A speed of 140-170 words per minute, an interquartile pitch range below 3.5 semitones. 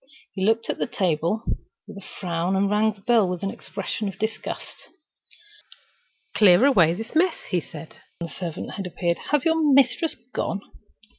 No: average, 165 wpm; average, 4.3 semitones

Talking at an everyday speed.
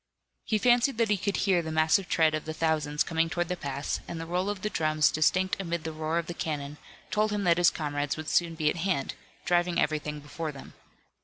No: fast, 230 wpm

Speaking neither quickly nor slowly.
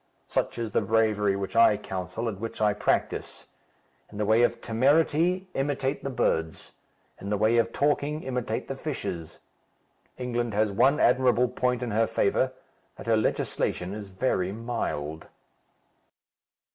Yes: average, 145 wpm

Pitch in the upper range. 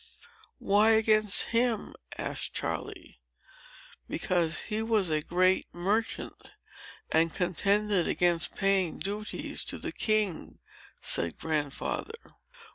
Yes: high, 195 Hz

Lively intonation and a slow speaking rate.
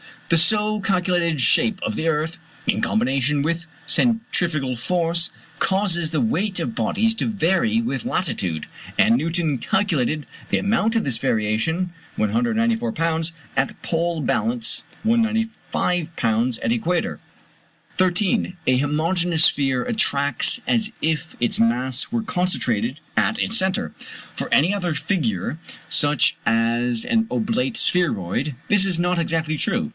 Yes: wide, 7.2 semitones; slow, 130 wpm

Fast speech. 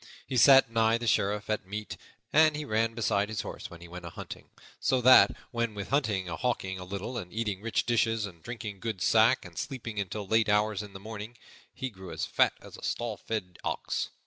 Yes: fast, 220 wpm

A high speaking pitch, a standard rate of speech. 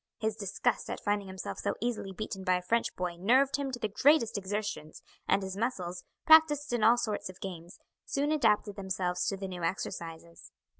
Yes: high, 200 Hz; average, 190 wpm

